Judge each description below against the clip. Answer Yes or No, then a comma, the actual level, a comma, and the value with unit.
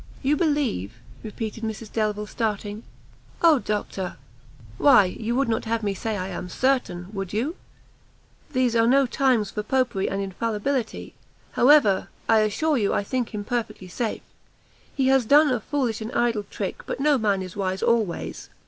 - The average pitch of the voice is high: Yes, high, 225 Hz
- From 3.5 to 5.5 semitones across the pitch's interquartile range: Yes, average, 4.2 semitones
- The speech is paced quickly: No, average, 165 wpm